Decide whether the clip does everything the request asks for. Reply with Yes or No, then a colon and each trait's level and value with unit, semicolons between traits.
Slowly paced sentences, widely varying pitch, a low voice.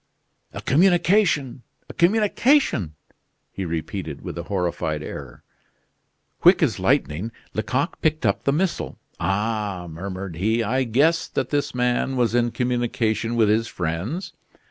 Yes: slow, 130 wpm; wide, 6.9 semitones; low, 115 Hz